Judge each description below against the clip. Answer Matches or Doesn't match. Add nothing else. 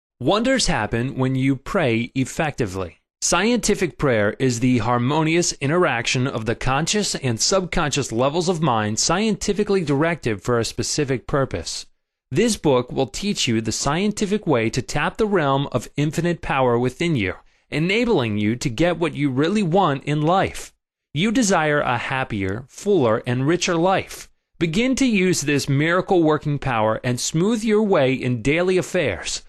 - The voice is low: Doesn't match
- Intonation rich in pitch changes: Matches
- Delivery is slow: Doesn't match